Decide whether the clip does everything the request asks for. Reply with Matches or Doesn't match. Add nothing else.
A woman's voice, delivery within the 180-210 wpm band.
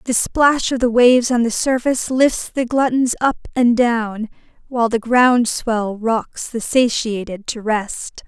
Doesn't match